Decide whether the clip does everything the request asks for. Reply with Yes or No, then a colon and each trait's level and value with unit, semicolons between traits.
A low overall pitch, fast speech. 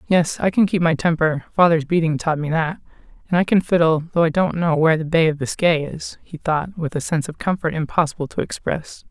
No: medium, 165 Hz; fast, 230 wpm